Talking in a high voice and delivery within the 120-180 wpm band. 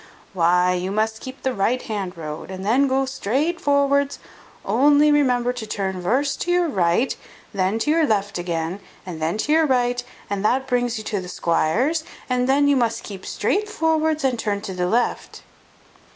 No: high, 240 Hz; average, 190 wpm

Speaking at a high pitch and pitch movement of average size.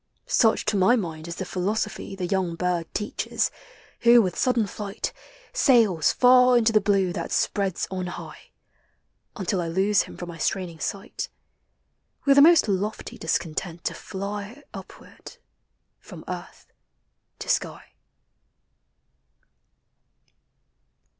Yes: high, 195 Hz; average, 3.8 semitones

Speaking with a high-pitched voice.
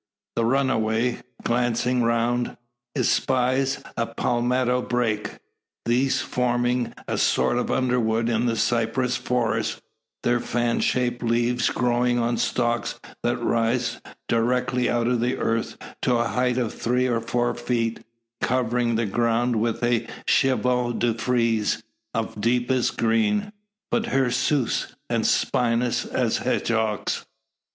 No: low, 120 Hz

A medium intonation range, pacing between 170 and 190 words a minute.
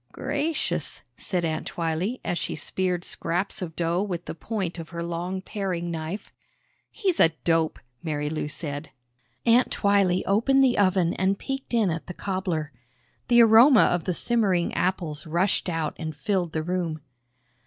No: average, 3.7 semitones; average, 155 wpm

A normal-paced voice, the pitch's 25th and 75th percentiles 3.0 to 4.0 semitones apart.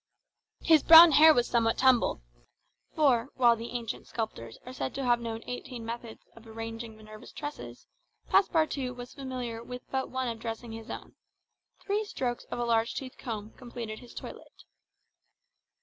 No: average, 160 wpm; narrow, 2.4 semitones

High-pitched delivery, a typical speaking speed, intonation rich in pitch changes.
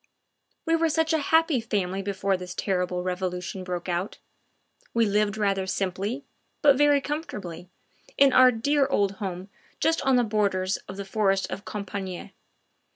Yes: high, 200 Hz; average, 155 wpm; wide, 6.0 semitones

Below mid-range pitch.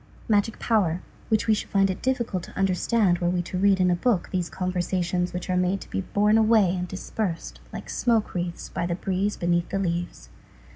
No: medium, 185 Hz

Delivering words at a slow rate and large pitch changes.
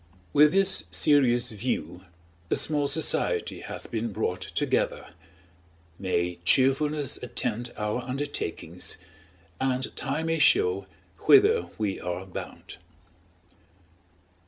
Yes: slow, 100 wpm; wide, 7.2 semitones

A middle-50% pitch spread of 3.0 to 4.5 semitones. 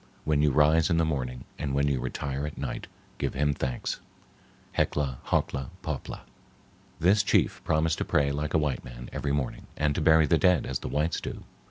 No: narrow, 2.4 semitones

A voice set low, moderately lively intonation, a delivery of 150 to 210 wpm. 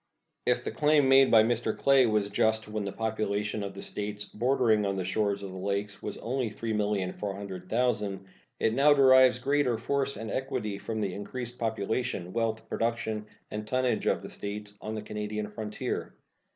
Yes: low, 110 Hz; average, 3.1 semitones; average, 165 wpm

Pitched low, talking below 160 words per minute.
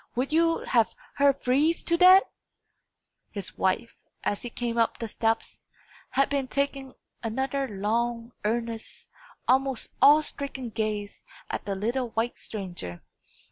No: high, 240 Hz; slow, 135 wpm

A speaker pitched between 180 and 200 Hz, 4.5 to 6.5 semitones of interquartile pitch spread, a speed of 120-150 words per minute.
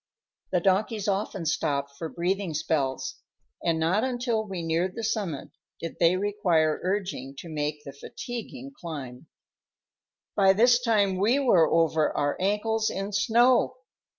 Yes: medium, 185 Hz; average, 5.3 semitones; average, 140 wpm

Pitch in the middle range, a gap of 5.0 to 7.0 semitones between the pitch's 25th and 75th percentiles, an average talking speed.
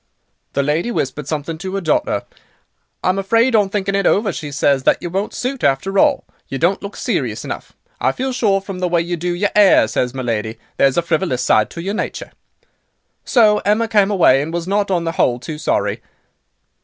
No: medium, 180 Hz; average, 5.3 semitones; fast, 210 wpm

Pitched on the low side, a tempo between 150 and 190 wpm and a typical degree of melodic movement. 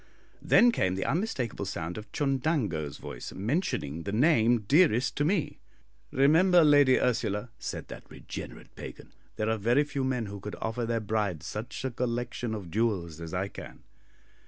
No: low, 115 Hz; average, 160 wpm; wide, 5.7 semitones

